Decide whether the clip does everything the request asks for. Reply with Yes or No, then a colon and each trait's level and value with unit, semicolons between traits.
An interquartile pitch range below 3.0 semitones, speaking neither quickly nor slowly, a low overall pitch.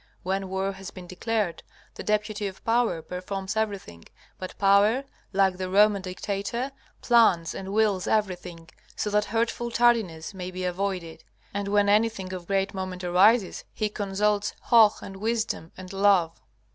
No: narrow, 2.4 semitones; average, 150 wpm; high, 195 Hz